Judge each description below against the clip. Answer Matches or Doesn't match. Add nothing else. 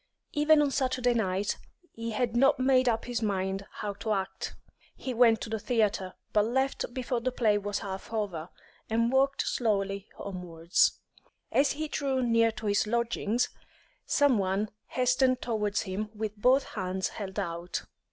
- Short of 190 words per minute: Matches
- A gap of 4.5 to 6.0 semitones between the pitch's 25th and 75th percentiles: Doesn't match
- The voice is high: Matches